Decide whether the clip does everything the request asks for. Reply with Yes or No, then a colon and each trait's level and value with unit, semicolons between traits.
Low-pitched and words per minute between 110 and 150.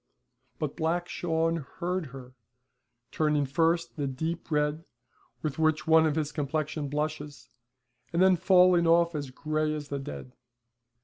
No: medium, 155 Hz; average, 140 wpm